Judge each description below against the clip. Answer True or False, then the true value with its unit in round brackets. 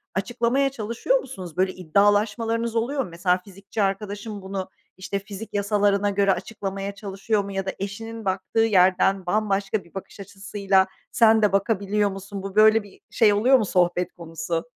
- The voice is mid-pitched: False (200 Hz)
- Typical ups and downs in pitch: False (2.2 semitones)